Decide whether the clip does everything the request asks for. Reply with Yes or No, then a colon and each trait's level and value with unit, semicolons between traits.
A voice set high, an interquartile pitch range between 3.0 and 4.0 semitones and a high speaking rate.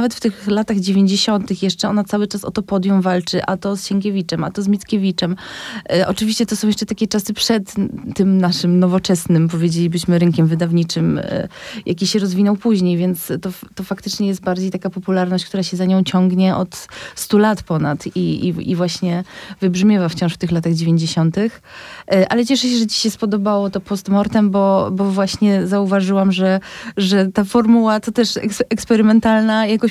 No: high, 195 Hz; narrow, 2.6 semitones; fast, 180 wpm